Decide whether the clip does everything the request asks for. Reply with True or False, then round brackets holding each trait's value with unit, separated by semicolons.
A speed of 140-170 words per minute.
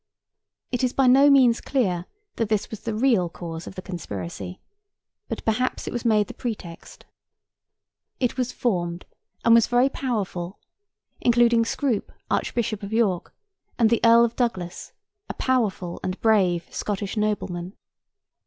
True (145 wpm)